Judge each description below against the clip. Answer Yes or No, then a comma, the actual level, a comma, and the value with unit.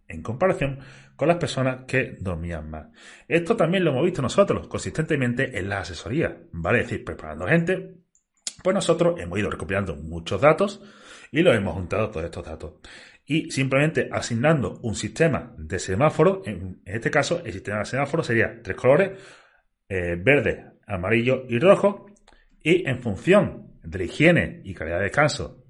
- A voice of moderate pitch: No, low, 125 Hz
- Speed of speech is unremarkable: Yes, average, 160 wpm